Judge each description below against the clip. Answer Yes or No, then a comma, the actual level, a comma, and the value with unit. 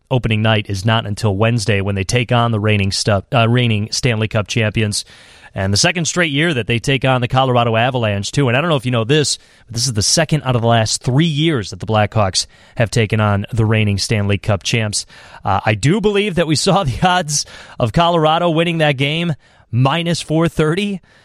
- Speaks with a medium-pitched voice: No, low, 120 Hz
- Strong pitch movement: Yes, wide, 6.1 semitones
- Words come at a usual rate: No, fast, 215 wpm